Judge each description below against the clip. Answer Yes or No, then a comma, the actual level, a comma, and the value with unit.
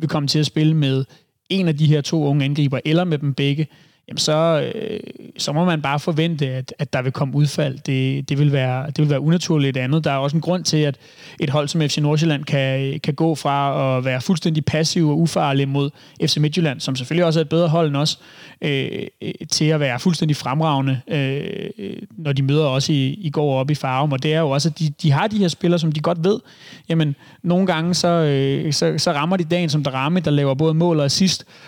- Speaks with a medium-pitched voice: Yes, medium, 155 Hz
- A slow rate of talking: No, fast, 235 wpm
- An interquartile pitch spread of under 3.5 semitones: Yes, average, 2.9 semitones